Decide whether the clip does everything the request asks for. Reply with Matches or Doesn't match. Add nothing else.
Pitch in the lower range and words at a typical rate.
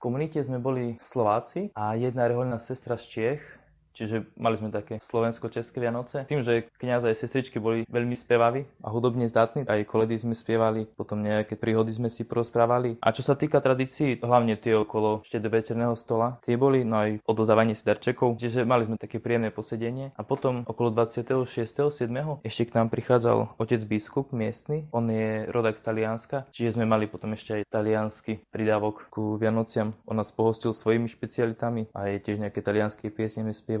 Doesn't match